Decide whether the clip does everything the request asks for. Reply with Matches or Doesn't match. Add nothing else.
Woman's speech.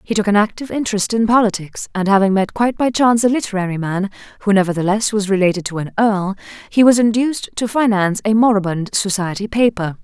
Matches